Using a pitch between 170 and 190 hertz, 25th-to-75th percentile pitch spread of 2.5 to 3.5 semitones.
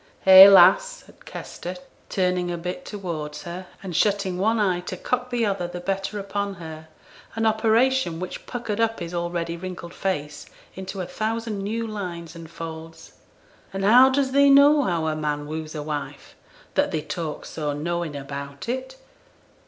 No: medium, 185 Hz; average, 4.9 semitones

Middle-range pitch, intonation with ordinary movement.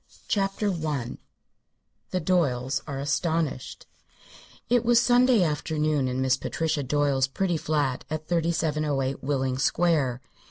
Yes: medium, 150 Hz; average, 4.2 semitones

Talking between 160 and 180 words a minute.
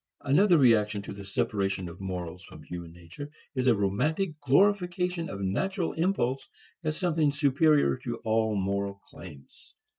No: average, 145 wpm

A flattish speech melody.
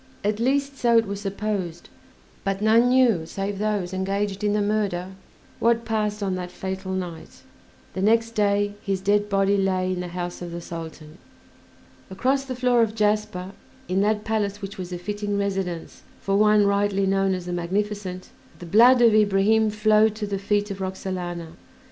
Yes: narrow, 2.2 semitones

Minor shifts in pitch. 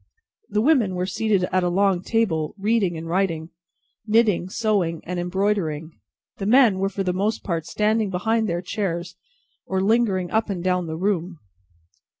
No: average, 3.3 semitones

